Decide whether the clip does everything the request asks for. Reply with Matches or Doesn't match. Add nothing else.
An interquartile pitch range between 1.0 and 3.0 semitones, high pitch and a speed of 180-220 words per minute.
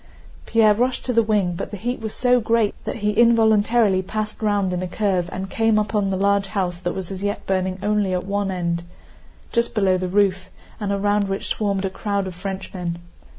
Matches